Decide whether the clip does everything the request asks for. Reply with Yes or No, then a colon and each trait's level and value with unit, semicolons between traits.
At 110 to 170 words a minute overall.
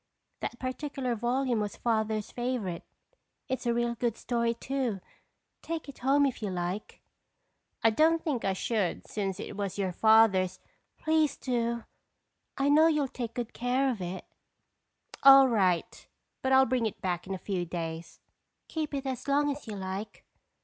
Yes: average, 165 wpm